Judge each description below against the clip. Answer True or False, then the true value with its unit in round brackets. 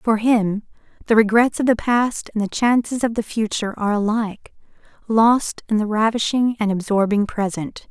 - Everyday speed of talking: True (165 wpm)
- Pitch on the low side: False (220 Hz)